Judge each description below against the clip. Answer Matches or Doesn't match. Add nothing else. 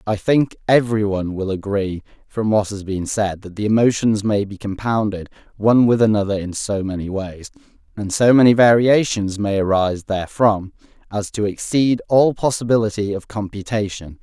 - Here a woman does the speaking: Doesn't match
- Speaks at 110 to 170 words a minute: Matches